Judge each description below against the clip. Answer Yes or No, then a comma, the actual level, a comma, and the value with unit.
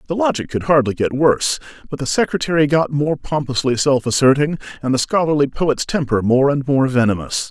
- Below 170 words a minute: No, average, 185 wpm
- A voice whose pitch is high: No, medium, 140 Hz